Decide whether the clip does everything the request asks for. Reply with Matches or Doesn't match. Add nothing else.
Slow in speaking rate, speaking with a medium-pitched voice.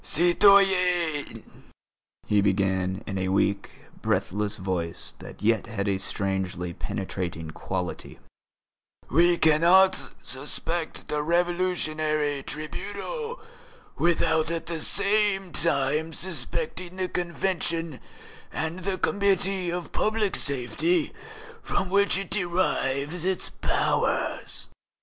Matches